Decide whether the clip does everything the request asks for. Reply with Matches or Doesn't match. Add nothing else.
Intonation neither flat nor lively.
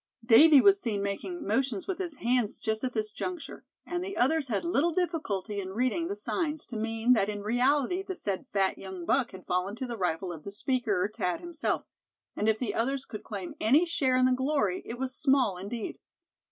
Doesn't match